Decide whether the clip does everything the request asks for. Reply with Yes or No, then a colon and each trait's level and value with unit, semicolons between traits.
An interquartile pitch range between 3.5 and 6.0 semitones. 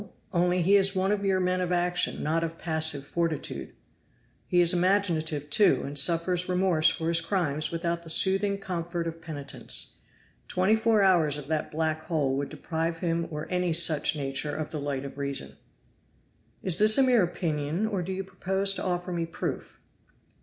No: average, 3.1 semitones